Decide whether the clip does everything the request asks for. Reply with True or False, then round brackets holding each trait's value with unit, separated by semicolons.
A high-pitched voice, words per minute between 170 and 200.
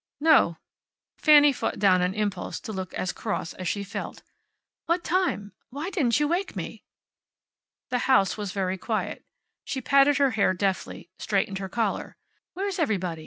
False (215 Hz; 160 wpm)